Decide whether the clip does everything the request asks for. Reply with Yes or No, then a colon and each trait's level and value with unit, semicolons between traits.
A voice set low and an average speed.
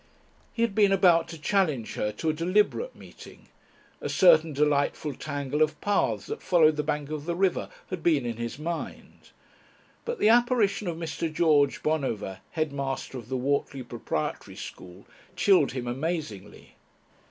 No: medium, 155 Hz; average, 155 wpm